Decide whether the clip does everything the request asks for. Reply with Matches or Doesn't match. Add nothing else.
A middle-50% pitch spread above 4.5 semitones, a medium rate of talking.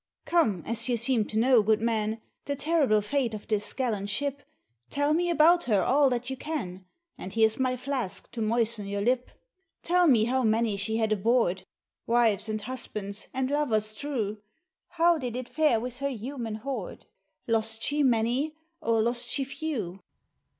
Doesn't match